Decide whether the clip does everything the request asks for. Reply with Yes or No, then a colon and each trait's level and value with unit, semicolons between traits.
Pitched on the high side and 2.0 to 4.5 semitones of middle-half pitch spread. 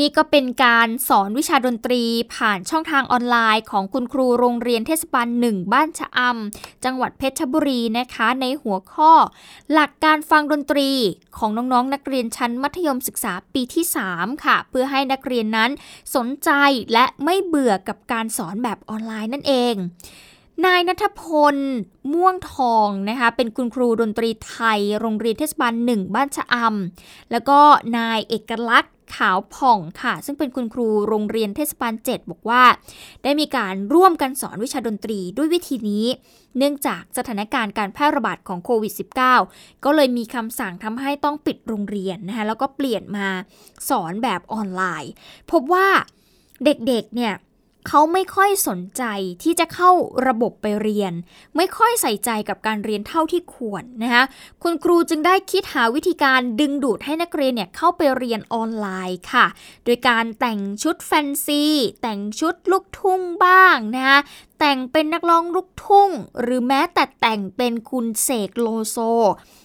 No: very high, 250 Hz; average, 4.9 semitones